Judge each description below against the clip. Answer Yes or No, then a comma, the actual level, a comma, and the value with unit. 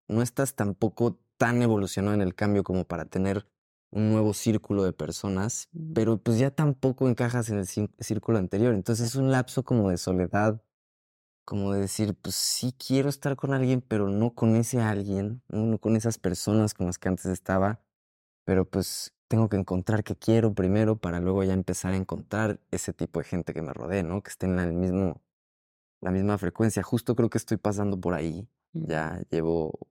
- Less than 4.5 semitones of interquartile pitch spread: Yes, average, 3.7 semitones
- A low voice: Yes, low, 105 Hz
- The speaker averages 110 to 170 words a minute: No, fast, 190 wpm